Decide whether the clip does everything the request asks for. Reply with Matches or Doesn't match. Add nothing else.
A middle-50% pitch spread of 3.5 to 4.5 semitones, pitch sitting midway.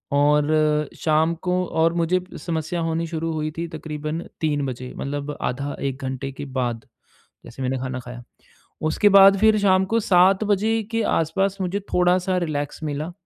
Matches